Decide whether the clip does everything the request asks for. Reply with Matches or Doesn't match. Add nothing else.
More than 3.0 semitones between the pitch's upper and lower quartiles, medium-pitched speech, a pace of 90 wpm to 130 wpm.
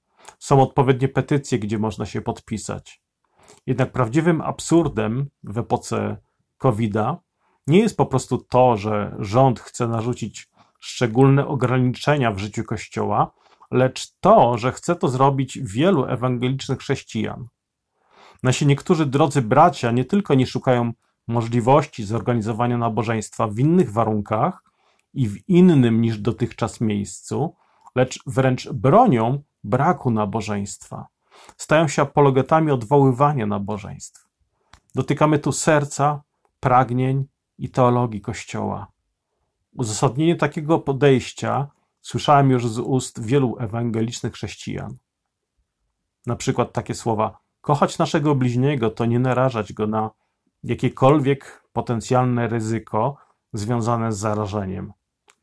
Doesn't match